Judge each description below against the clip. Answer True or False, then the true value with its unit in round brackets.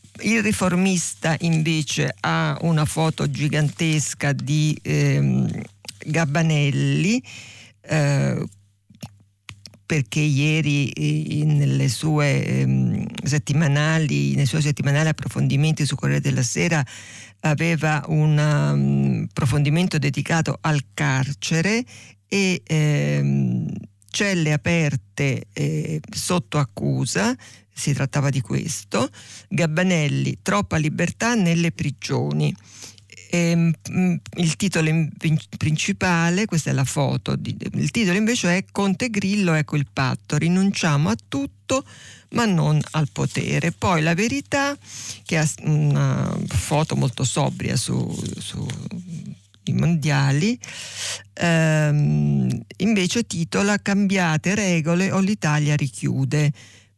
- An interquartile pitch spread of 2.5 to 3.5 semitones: False (4.6 semitones)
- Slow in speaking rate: True (95 wpm)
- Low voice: False (150 Hz)